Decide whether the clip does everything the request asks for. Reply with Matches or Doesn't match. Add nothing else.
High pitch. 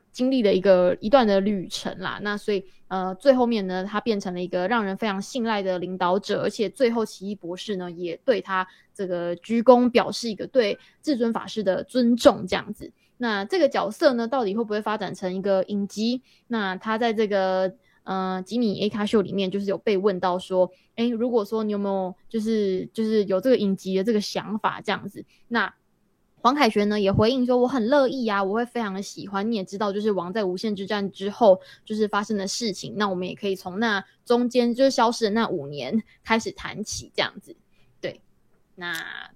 Matches